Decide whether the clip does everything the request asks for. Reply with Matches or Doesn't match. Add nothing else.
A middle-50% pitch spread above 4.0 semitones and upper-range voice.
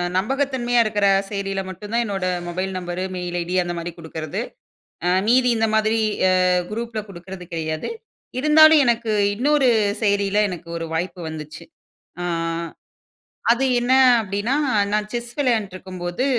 Matches